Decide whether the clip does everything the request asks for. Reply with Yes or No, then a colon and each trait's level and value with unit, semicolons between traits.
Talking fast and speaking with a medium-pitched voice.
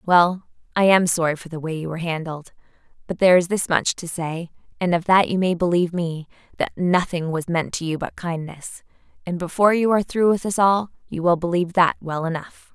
Yes: fast, 215 wpm; medium, 175 Hz